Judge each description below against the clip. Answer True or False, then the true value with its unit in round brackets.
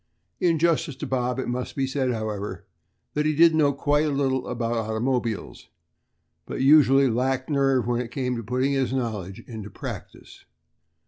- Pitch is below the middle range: True (130 Hz)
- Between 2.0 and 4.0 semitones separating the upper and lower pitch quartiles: True (2.9 semitones)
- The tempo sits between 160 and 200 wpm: True (170 wpm)